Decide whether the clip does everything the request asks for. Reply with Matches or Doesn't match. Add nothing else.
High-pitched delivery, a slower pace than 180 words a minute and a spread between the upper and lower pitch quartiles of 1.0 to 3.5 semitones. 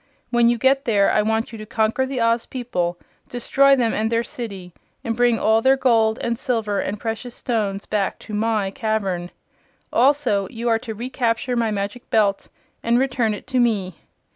Doesn't match